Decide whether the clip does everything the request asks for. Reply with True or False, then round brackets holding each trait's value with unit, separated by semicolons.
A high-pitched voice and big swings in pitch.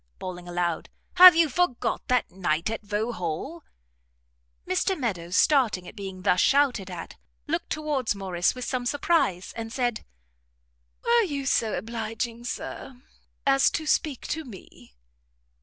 True (230 Hz; 7.1 semitones)